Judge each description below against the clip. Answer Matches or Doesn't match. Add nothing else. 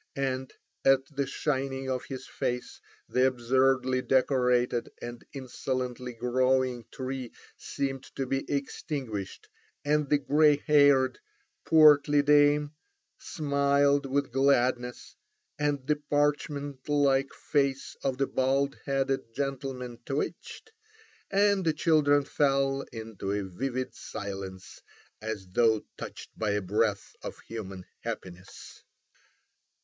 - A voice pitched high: Doesn't match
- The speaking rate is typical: Doesn't match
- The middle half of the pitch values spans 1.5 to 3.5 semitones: Matches